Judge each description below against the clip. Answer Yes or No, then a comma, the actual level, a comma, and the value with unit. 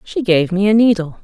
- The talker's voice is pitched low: No, high, 195 Hz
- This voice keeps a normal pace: No, fast, 245 wpm